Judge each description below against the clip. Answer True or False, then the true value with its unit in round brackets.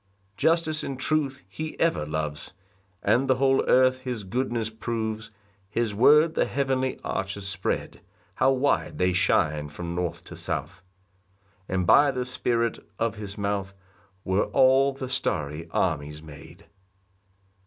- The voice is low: True (115 Hz)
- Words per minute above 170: False (140 wpm)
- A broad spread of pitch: True (6.5 semitones)